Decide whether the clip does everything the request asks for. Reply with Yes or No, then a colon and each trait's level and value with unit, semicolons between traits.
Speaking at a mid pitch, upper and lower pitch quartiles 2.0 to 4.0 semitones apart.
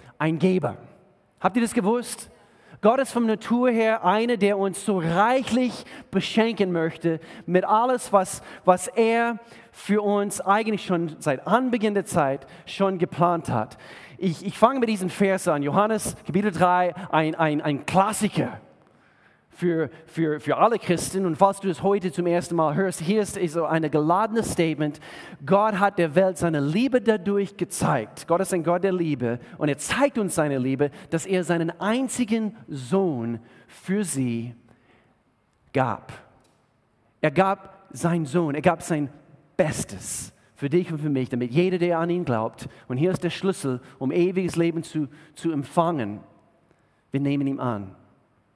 No: medium, 175 Hz; average, 4.8 semitones